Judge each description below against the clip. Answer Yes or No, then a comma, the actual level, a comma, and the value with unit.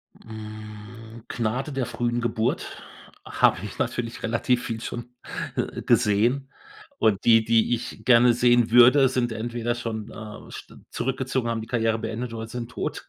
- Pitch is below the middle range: Yes, low, 115 Hz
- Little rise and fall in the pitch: Yes, narrow, 1.6 semitones